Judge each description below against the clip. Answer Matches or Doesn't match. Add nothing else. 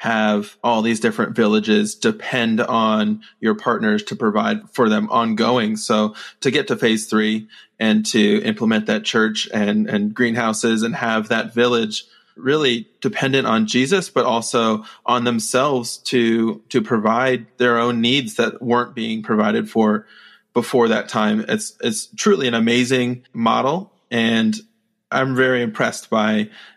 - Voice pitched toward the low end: Matches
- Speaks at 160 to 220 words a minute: Doesn't match